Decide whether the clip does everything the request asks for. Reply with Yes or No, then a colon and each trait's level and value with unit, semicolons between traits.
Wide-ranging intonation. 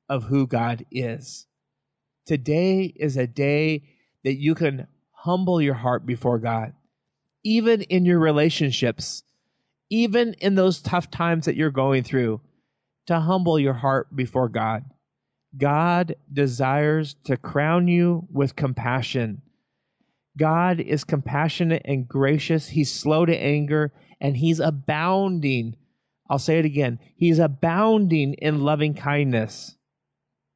No: average, 3.7 semitones